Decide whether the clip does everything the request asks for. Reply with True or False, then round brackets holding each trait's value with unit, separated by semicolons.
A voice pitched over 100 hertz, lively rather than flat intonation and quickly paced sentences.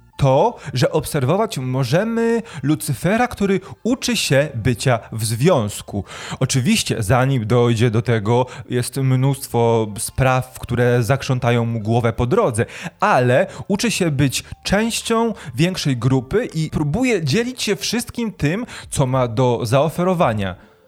False (135 Hz; 6.7 semitones; 120 wpm)